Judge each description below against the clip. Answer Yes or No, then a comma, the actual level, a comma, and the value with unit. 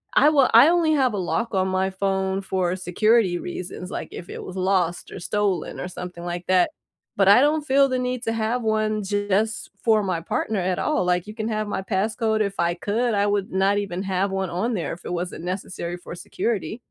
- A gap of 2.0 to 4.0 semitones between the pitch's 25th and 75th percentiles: Yes, average, 3.4 semitones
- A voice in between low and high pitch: No, high, 195 Hz